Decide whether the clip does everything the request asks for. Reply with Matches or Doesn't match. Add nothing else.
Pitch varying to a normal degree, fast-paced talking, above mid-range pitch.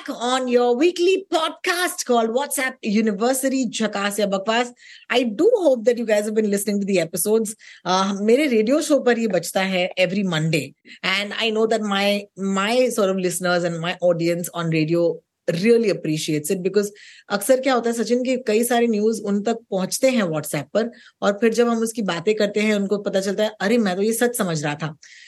Matches